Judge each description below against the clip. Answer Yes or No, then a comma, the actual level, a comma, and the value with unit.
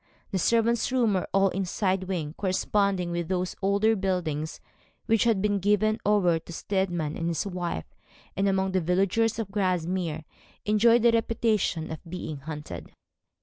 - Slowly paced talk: No, average, 160 wpm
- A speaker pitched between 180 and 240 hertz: Yes, high, 190 Hz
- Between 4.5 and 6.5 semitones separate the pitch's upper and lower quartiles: No, average, 3.4 semitones